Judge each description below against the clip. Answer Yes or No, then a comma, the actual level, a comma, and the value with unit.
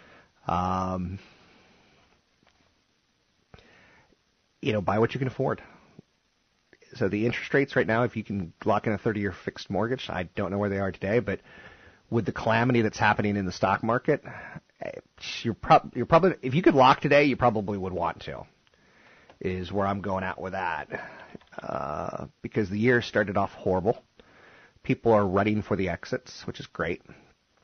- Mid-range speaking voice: No, low, 105 Hz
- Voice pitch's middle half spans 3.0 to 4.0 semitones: Yes, average, 3.4 semitones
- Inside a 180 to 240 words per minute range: No, average, 165 wpm